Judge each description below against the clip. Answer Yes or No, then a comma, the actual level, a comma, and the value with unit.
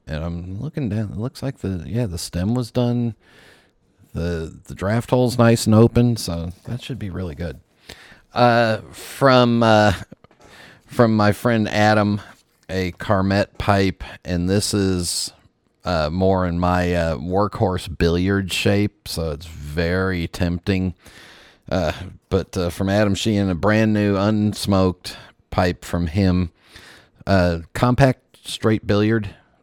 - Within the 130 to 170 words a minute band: Yes, average, 140 wpm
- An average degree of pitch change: Yes, average, 3.9 semitones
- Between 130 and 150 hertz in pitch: No, low, 100 Hz